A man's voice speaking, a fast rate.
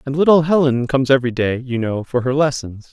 Yes: male; fast, 225 wpm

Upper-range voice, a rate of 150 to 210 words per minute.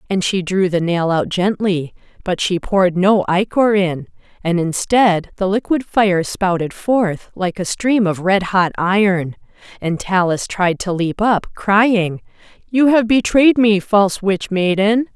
Yes: high, 195 Hz; average, 160 wpm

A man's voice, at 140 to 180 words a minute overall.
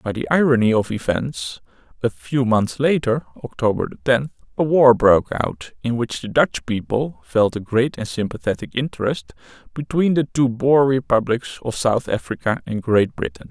Yes: male; average, 165 wpm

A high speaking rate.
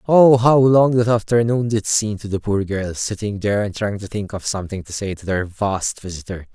Yes: fast, 230 wpm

